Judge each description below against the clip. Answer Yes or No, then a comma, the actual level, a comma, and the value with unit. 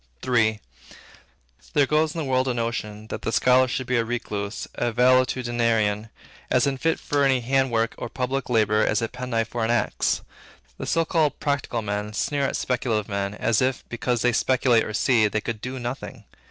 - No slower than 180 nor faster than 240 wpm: Yes, average, 185 wpm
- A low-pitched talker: Yes, low, 120 Hz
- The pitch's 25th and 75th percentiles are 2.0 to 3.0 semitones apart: Yes, average, 2.7 semitones